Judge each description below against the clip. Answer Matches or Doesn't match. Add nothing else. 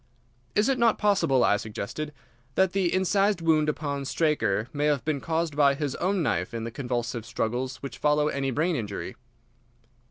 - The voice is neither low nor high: Matches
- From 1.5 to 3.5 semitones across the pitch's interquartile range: Doesn't match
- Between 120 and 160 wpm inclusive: Doesn't match